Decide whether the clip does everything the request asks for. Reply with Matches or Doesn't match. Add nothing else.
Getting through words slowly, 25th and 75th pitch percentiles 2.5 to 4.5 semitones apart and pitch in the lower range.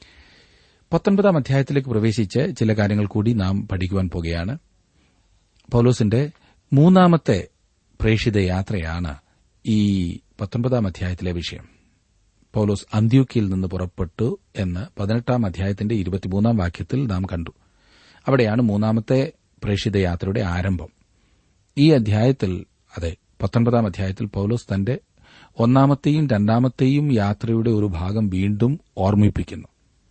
Doesn't match